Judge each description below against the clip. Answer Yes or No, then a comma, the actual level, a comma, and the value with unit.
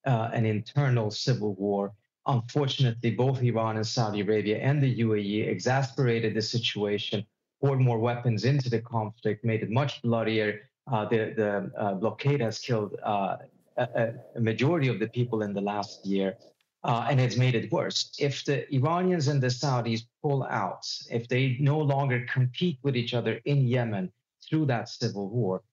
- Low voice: Yes, low, 120 Hz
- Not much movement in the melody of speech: No, average, 3.6 semitones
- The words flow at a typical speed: Yes, average, 170 wpm